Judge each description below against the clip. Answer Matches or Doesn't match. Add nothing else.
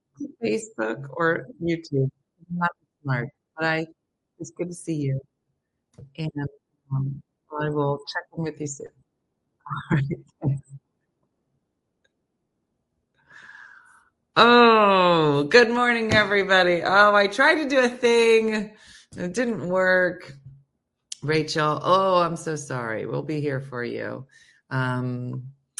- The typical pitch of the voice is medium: Matches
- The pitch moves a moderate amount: Doesn't match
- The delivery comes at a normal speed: Doesn't match